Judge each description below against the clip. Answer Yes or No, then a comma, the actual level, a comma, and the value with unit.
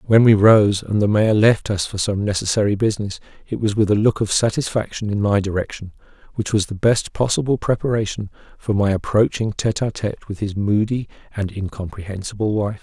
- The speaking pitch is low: Yes, low, 105 Hz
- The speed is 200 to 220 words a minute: No, average, 185 wpm